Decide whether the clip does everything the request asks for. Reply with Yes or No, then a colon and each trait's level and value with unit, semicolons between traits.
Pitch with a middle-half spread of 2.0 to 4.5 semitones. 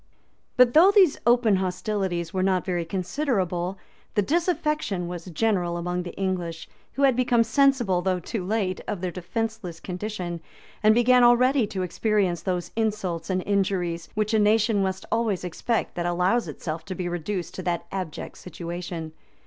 Yes: average, 4.2 semitones